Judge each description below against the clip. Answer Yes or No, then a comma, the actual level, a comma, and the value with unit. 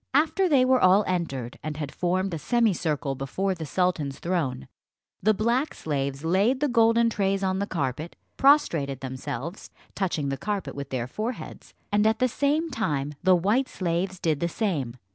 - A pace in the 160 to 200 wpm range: Yes, average, 170 wpm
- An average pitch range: No, wide, 7.3 semitones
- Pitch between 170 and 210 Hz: Yes, medium, 185 Hz